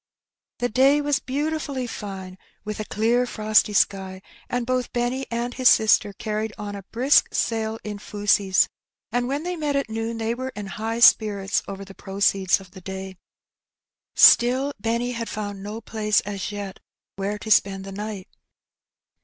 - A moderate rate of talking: Yes, average, 165 wpm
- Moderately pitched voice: No, high, 215 Hz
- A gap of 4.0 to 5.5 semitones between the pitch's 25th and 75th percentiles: No, average, 3.5 semitones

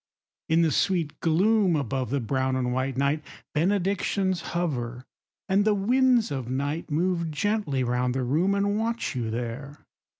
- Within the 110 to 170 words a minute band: Yes, average, 155 wpm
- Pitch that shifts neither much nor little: No, wide, 7.0 semitones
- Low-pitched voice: No, medium, 155 Hz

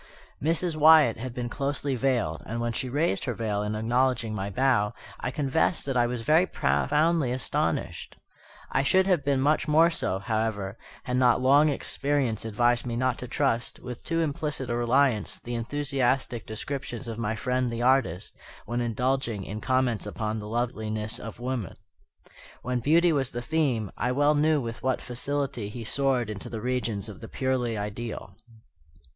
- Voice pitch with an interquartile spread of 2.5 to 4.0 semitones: Yes, average, 3.6 semitones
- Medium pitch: No, low, 125 Hz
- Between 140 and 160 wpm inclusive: No, average, 170 wpm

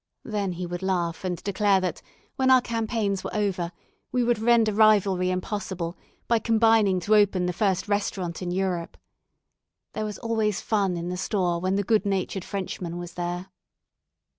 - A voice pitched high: Yes, high, 195 Hz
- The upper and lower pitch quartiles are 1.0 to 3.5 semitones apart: Yes, average, 3.1 semitones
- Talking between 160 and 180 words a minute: Yes, average, 165 wpm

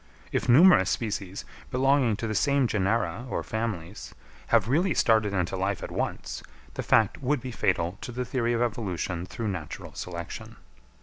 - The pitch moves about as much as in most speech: Yes, average, 4.4 semitones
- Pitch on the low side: Yes, low, 110 Hz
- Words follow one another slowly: No, average, 165 wpm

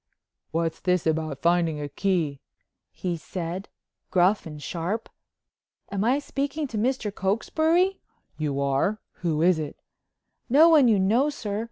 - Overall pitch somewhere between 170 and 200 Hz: Yes, medium, 185 Hz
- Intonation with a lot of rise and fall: Yes, wide, 6.4 semitones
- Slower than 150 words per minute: Yes, average, 140 wpm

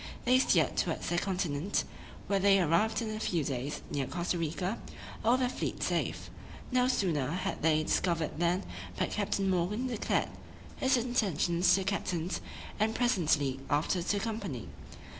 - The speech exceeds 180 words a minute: No, average, 160 wpm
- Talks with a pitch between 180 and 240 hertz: Yes, medium, 185 Hz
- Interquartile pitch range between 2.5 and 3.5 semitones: No, average, 4.8 semitones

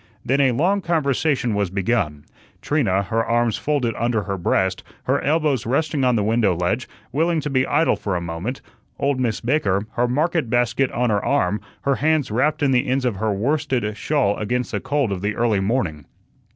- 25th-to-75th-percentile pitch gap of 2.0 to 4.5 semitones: No, average, 5.3 semitones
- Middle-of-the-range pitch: No, low, 120 Hz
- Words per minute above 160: Yes, average, 190 wpm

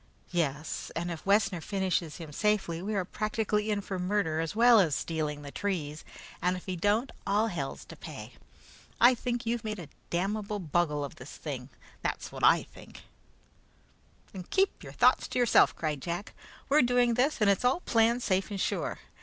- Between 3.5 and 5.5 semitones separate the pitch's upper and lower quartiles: Yes, average, 4.9 semitones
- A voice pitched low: No, high, 195 Hz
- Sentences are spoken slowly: No, average, 185 wpm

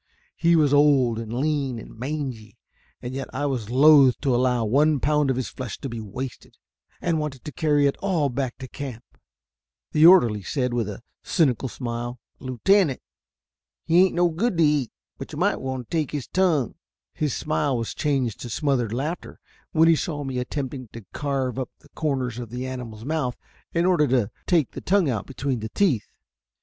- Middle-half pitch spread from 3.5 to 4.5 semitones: Yes, average, 3.8 semitones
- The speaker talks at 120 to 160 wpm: No, average, 185 wpm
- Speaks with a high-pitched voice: No, low, 135 Hz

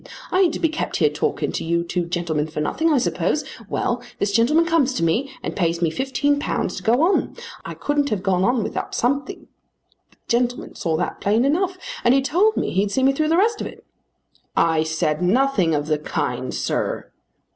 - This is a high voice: Yes, high, 240 Hz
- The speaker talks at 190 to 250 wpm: Yes, fast, 205 wpm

